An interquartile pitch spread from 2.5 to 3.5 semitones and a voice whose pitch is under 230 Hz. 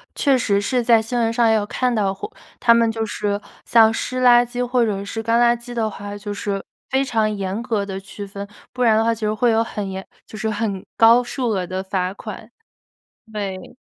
Yes: average, 2.8 semitones; high, 220 Hz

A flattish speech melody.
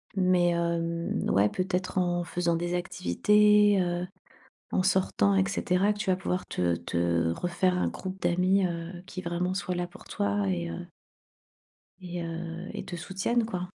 Yes: narrow, 1.7 semitones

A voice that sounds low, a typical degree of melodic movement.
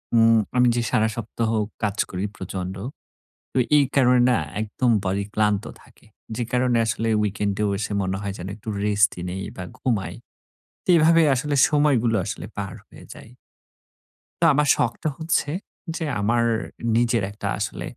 Yes: low, 115 Hz; average, 3.7 semitones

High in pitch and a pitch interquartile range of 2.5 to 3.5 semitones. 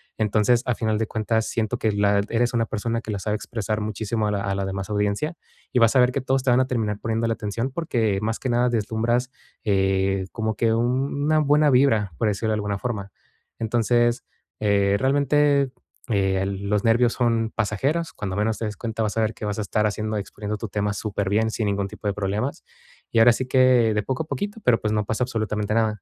No: low, 110 Hz; average, 2.8 semitones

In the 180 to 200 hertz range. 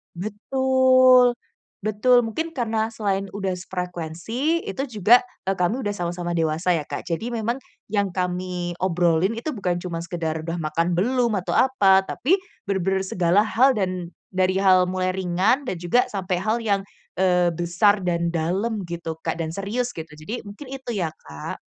Yes: high, 190 Hz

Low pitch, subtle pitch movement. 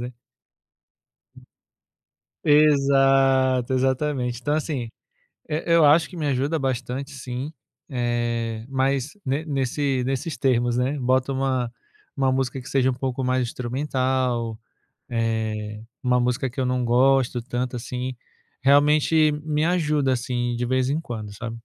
Yes: low, 130 Hz; narrow, 2.3 semitones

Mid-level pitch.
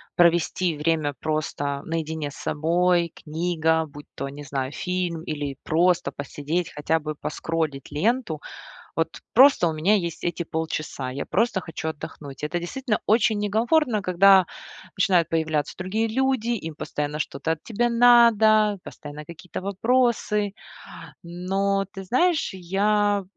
Yes: medium, 170 Hz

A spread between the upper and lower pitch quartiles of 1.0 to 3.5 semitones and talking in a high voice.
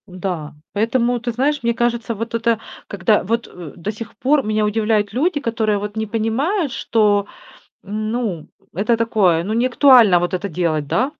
Yes: average, 2.9 semitones; high, 220 Hz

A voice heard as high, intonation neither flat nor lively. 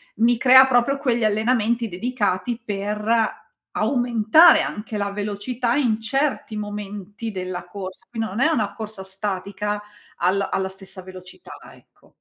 Yes: high, 210 Hz; average, 3.2 semitones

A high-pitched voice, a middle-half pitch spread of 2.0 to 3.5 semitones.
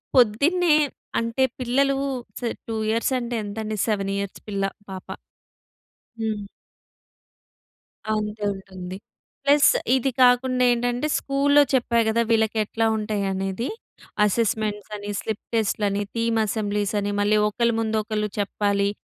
Yes: high, 220 Hz; average, 2.9 semitones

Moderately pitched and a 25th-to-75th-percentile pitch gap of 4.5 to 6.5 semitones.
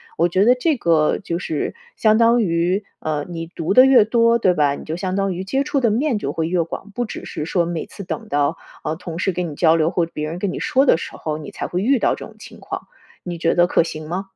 Yes: medium, 175 Hz; average, 4.9 semitones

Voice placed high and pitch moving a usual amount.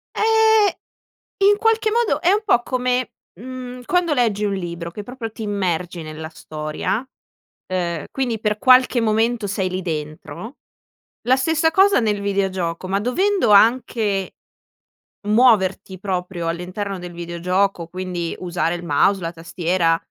No: high, 200 Hz; wide, 6.3 semitones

